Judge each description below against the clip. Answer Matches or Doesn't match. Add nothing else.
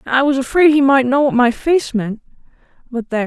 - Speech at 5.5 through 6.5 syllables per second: Matches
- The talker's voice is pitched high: Matches